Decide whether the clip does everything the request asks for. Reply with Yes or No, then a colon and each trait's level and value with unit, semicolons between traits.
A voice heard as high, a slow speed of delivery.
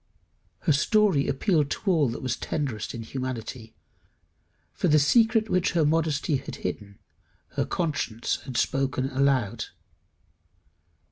No: medium, 140 Hz; slow, 125 wpm